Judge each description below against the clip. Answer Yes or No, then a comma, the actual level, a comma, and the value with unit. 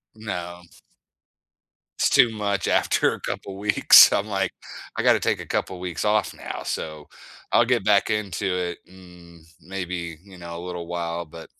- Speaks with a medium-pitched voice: No, very low, 90 Hz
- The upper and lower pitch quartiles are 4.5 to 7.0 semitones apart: No, average, 2.7 semitones